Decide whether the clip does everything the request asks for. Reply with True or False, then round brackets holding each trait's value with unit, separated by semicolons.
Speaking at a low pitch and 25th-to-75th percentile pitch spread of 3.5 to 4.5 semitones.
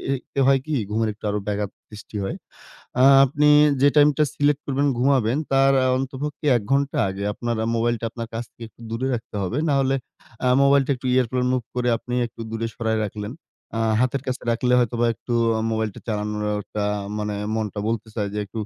True (120 Hz; 3.8 semitones)